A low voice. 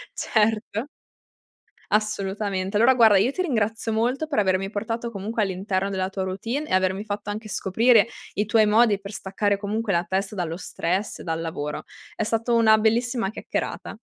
No: high, 210 Hz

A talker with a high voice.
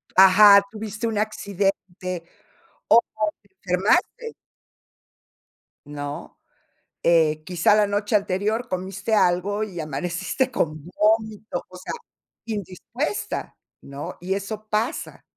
Yes: high, 200 Hz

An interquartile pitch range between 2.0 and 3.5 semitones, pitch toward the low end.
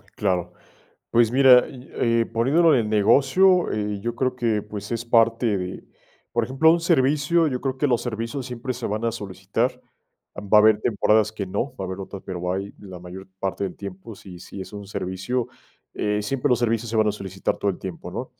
No: average, 4.2 semitones; low, 110 Hz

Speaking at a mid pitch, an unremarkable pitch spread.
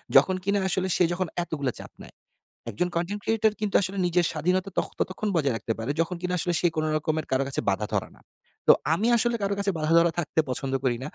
Yes: medium, 175 Hz; average, 3.9 semitones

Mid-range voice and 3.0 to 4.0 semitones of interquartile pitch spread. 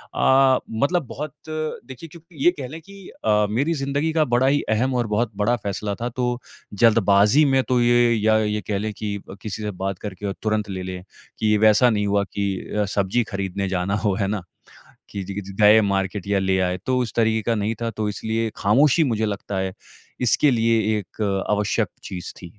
No: low, 110 Hz; average, 3.7 semitones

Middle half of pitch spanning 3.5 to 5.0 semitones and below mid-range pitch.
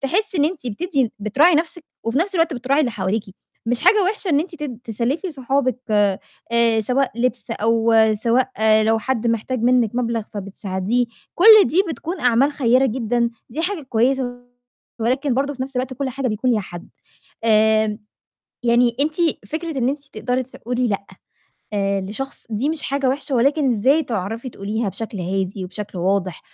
No: average, 4.2 semitones; high, 245 Hz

